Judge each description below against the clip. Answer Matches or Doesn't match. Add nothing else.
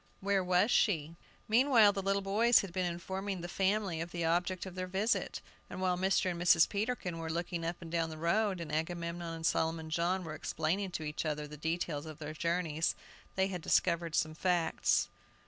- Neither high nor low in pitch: Matches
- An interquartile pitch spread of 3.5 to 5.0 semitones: Doesn't match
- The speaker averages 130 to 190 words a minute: Doesn't match